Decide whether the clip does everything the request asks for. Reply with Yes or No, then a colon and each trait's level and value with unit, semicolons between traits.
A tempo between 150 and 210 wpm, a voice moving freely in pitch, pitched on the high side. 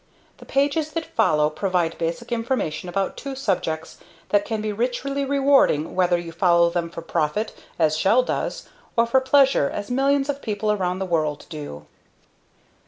Yes: average, 165 wpm; wide, 7.9 semitones; high, 200 Hz